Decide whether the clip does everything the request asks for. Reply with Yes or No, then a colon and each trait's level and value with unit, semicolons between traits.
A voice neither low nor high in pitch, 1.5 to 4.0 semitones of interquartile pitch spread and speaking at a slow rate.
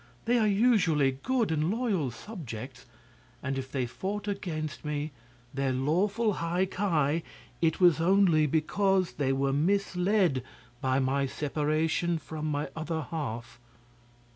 No: medium, 160 Hz; wide, 5.6 semitones; slow, 130 wpm